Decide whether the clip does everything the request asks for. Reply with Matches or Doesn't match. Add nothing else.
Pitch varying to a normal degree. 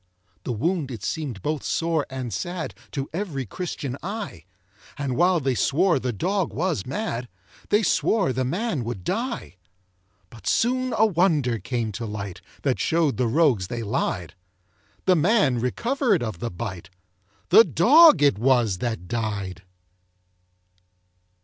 Doesn't match